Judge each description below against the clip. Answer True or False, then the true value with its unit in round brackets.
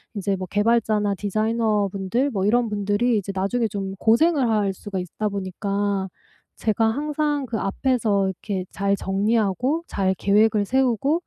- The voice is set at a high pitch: True (210 Hz)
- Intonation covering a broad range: False (3.0 semitones)